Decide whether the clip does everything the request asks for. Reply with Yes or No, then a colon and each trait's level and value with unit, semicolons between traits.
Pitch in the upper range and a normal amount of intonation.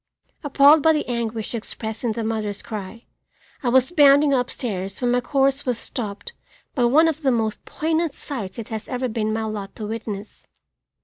Yes: high, 240 Hz; average, 4.1 semitones